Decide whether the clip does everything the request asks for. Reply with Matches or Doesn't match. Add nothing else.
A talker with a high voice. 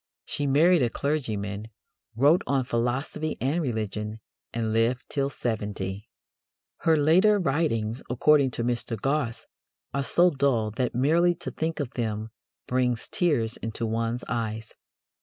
Doesn't match